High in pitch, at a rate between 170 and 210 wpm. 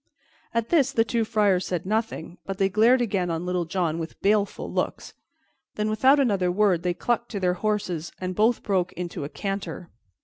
Yes: high, 195 Hz; average, 190 wpm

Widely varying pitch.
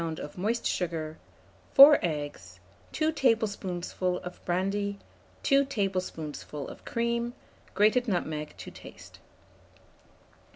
Yes: wide, 6.5 semitones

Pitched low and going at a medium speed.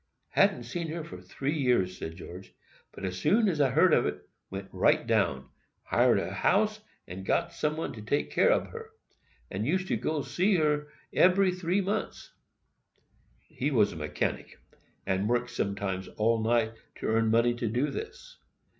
Yes: low, 125 Hz; average, 170 wpm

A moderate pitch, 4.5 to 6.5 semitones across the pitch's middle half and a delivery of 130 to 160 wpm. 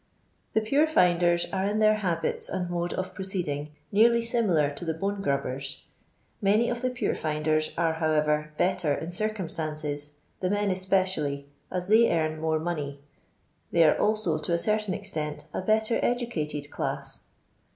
Yes: medium, 175 Hz; average, 5.1 semitones; average, 150 wpm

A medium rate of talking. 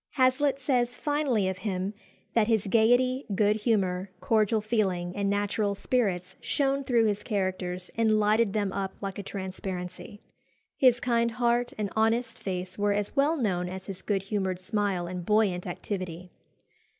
Yes: average, 155 wpm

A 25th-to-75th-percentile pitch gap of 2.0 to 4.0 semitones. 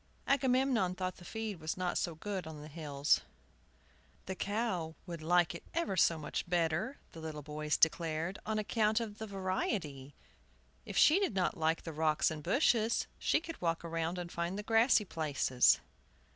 No: average, 4.9 semitones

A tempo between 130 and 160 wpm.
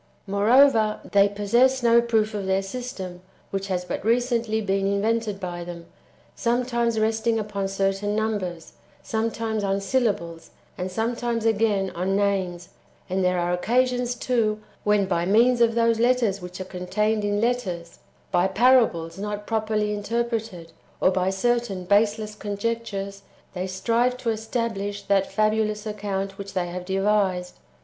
Yes: average, 145 wpm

